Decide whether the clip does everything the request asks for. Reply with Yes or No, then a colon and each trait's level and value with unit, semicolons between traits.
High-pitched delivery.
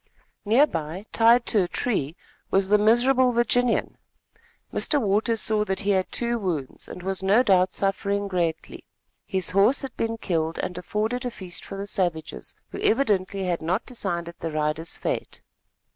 Yes: high, 195 Hz